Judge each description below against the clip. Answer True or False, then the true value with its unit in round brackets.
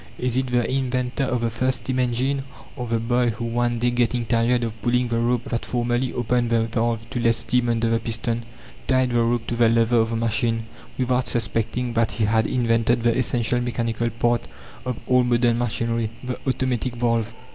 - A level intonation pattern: True (1.2 semitones)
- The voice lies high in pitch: False (120 Hz)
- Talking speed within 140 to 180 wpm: False (200 wpm)